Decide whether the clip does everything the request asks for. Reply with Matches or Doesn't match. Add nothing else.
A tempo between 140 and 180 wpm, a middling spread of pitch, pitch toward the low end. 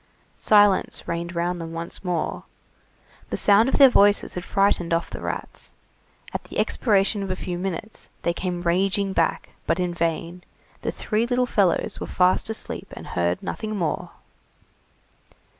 Doesn't match